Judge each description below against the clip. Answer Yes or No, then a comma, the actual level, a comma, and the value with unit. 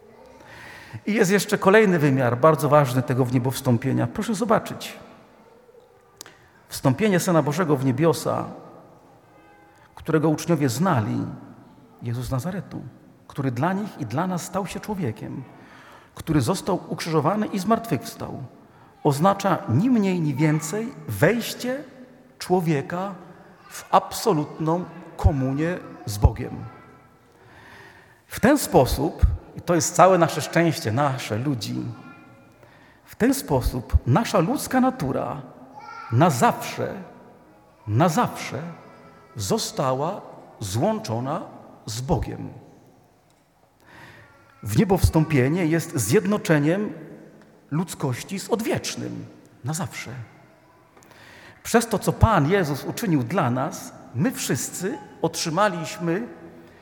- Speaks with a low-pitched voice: No, medium, 165 Hz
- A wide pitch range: Yes, wide, 6.1 semitones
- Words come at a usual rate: No, slow, 100 wpm